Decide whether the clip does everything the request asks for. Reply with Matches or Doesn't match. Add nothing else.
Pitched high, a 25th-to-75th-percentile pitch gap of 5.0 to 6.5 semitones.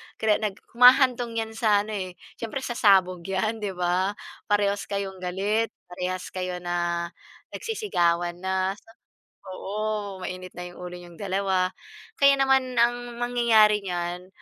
Doesn't match